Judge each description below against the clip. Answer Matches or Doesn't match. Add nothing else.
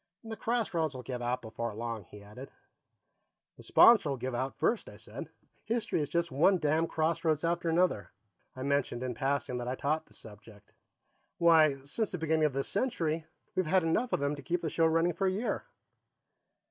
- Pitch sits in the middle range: Matches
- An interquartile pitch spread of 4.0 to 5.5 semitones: Matches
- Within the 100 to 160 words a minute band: Doesn't match